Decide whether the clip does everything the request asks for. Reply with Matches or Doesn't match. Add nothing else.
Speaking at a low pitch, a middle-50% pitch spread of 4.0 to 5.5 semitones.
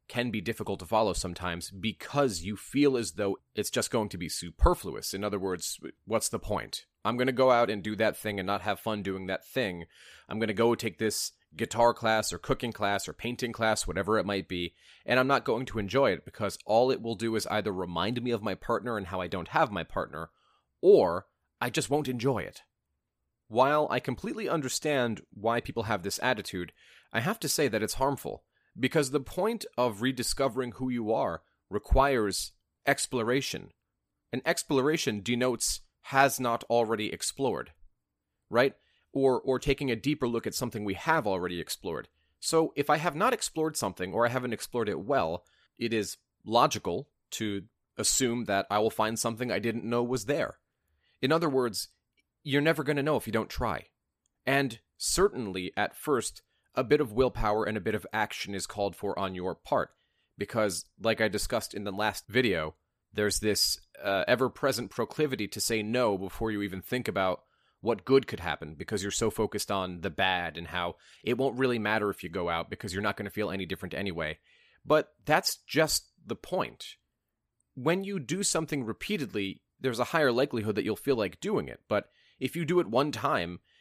Matches